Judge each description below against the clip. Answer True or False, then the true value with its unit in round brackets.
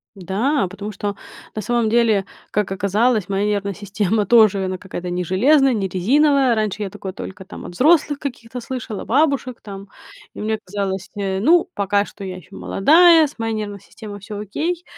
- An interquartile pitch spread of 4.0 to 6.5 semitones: True (4.3 semitones)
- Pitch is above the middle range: True (210 Hz)